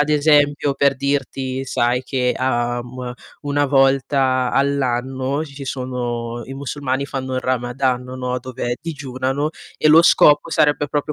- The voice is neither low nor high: No, low, 130 Hz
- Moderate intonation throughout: No, narrow, 2.1 semitones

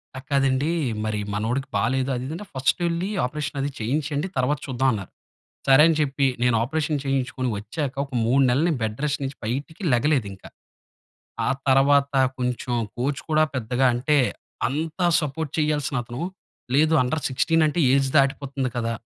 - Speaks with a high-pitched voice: No, low, 135 Hz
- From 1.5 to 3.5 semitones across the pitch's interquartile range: Yes, average, 3.1 semitones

